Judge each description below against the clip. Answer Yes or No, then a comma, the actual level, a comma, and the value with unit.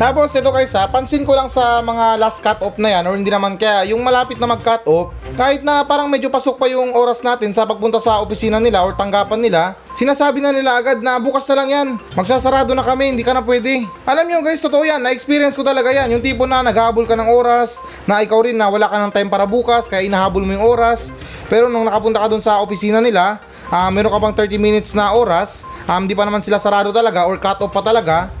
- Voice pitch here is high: Yes, high, 230 Hz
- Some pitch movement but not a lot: Yes, average, 3.8 semitones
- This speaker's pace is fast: Yes, fast, 245 wpm